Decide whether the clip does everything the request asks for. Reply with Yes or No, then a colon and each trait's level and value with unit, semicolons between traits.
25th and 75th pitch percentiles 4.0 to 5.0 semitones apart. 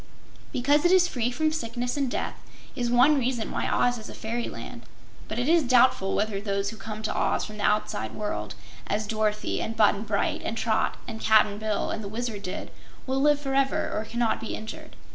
No: average, 3.4 semitones